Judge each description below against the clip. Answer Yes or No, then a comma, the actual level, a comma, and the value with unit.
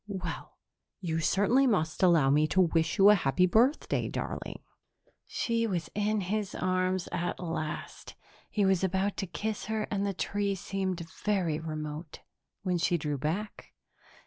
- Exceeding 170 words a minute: No, average, 150 wpm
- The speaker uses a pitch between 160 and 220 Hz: Yes, medium, 185 Hz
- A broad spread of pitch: No, average, 3.8 semitones